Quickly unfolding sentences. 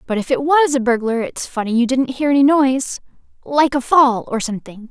Yes: fast, 210 wpm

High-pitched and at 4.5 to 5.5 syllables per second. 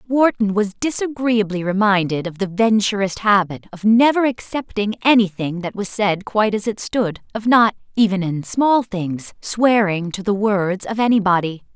Yes: high, 210 Hz; 4.7 syllables/s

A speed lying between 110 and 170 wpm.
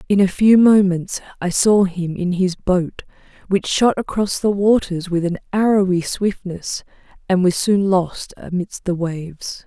Yes: average, 160 wpm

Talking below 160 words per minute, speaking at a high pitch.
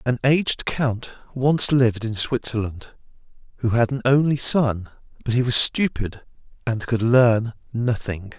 No: average, 145 wpm; low, 120 Hz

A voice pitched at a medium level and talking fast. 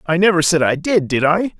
Yes: medium, 175 Hz; fast, 265 wpm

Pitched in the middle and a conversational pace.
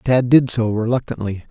No: low, 115 Hz; average, 160 wpm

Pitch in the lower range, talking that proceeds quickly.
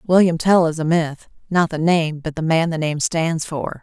No: medium, 165 Hz; fast, 220 wpm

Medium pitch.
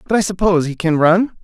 Yes: medium, 180 Hz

